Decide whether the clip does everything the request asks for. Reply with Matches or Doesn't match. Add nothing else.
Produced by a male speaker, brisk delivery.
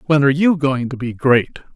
Matches